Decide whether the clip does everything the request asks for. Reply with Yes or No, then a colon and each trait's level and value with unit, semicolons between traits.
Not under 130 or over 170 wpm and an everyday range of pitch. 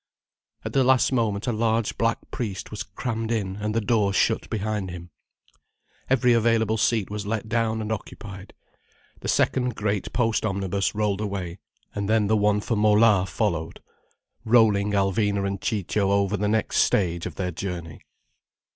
No: average, 160 wpm; narrow, 2.2 semitones